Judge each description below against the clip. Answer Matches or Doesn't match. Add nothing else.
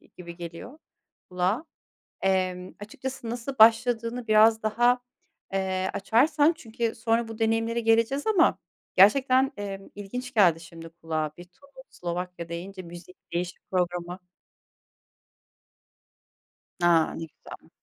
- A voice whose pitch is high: Matches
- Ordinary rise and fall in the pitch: Matches